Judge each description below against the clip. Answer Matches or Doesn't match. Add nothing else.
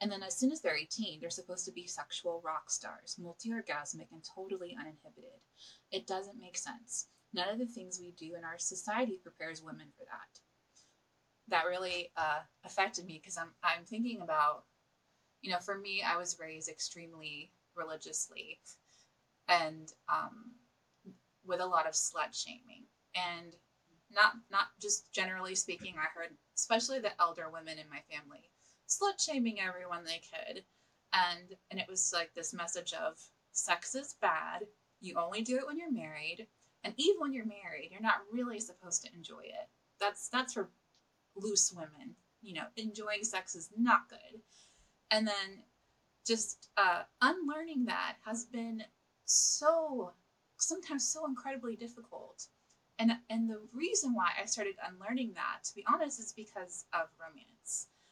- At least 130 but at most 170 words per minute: Matches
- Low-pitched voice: Doesn't match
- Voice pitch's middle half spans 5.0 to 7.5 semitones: Matches